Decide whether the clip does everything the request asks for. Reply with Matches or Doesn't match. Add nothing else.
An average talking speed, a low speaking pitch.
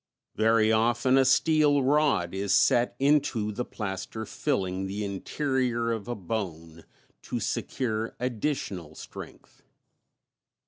Doesn't match